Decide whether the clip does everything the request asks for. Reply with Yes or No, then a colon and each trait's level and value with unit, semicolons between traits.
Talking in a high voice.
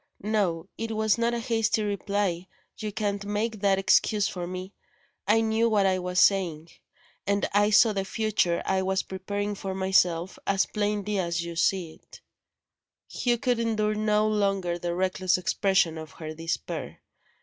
Yes: high, 200 Hz